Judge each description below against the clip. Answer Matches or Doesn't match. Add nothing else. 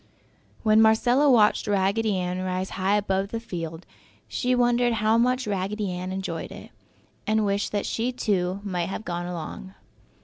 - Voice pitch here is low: Doesn't match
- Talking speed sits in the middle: Matches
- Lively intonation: Doesn't match